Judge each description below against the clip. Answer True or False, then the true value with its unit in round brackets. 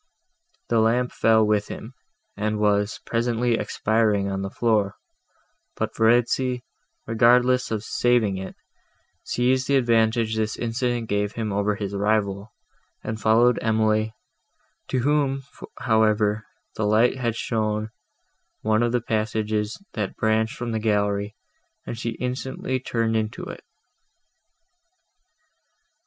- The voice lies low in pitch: True (110 Hz)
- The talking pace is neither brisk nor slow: False (120 wpm)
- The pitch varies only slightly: True (2.1 semitones)